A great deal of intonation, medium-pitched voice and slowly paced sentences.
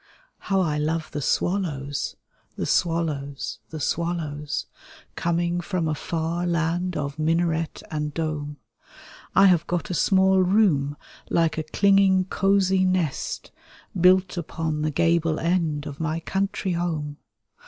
No: average, 3.2 semitones; medium, 165 Hz; slow, 130 wpm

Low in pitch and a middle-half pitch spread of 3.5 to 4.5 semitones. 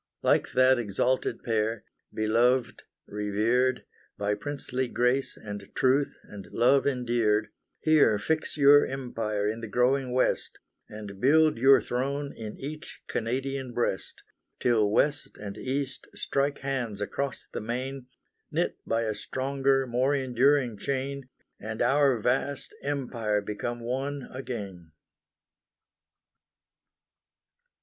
Yes: low, 125 Hz; average, 3.9 semitones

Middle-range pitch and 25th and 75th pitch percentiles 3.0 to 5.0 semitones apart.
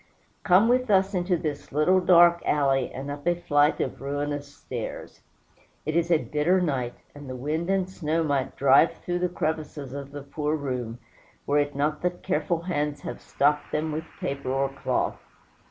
Yes: medium, 150 Hz; average, 3.5 semitones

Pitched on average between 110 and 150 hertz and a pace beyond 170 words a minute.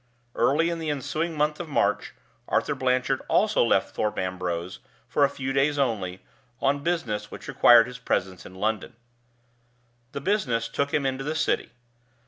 No: low, 135 Hz; average, 160 wpm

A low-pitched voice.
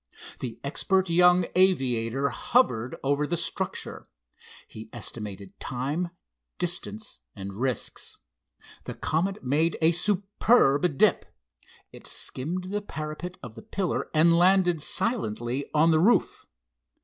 No: medium, 160 Hz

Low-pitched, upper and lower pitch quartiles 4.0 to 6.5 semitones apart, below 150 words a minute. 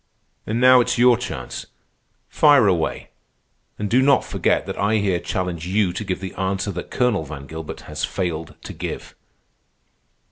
No: very low, 95 Hz; wide, 5.5 semitones; average, 165 wpm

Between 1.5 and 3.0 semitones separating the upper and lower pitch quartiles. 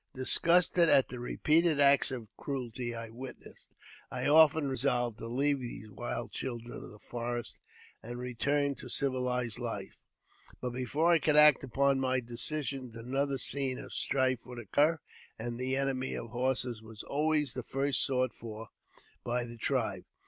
Yes: average, 2.7 semitones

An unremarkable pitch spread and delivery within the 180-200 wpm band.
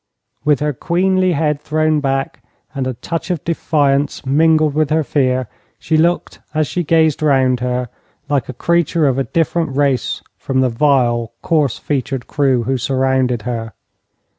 No: average, 3.3 semitones; average, 160 wpm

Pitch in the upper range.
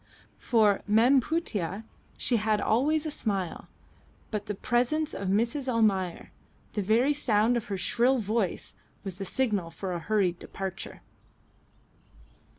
Yes: high, 215 Hz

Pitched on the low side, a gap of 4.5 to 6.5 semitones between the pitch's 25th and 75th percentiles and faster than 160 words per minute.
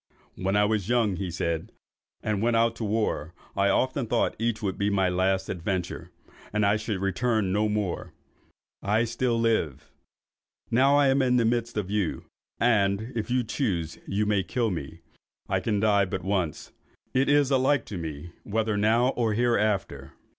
No: low, 105 Hz; average, 3.5 semitones; average, 175 wpm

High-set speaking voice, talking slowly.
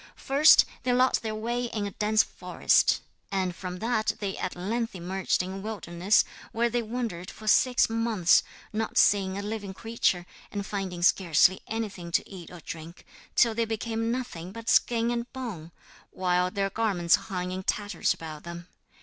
No: high, 205 Hz; average, 170 wpm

